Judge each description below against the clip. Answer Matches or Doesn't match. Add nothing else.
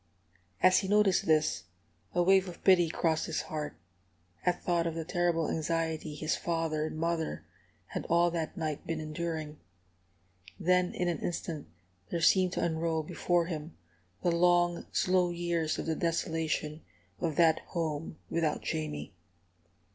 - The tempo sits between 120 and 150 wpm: Matches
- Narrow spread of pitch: Matches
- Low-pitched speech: Doesn't match